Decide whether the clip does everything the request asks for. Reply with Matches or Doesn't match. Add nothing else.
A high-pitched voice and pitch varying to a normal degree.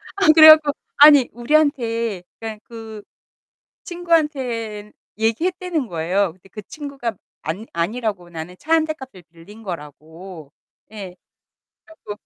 Doesn't match